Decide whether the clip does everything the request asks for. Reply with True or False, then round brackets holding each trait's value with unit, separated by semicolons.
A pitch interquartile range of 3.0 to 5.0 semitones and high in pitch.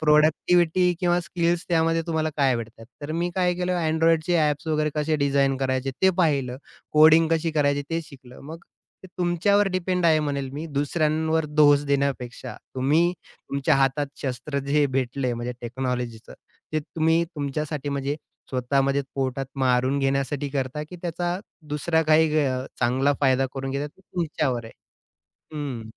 False (3.3 semitones; 145 Hz)